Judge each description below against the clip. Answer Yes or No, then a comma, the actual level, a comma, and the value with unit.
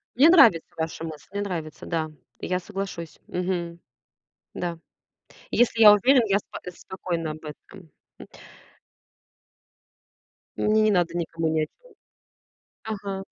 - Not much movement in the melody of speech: No, average, 4.0 semitones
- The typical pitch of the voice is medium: Yes, medium, 180 Hz